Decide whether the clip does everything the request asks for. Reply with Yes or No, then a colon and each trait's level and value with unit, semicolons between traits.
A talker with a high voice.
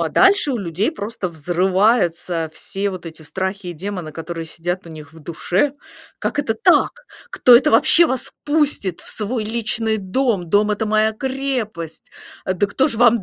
Yes: high, 205 Hz